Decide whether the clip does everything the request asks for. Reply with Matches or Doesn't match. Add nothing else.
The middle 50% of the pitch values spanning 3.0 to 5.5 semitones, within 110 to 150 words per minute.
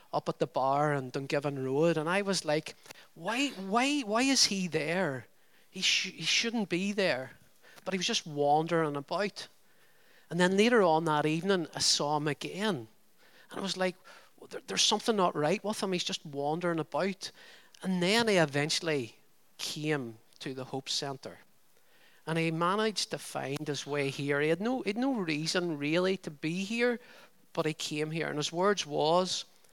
Doesn't match